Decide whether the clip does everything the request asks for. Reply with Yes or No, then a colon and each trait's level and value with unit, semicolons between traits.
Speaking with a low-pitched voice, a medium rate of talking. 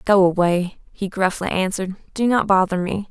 No: high, 190 Hz; average, 175 wpm